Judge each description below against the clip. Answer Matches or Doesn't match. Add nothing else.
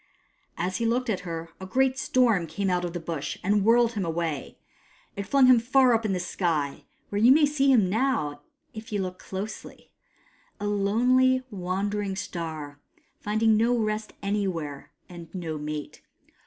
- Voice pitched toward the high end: Matches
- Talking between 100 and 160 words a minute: Doesn't match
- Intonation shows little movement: Doesn't match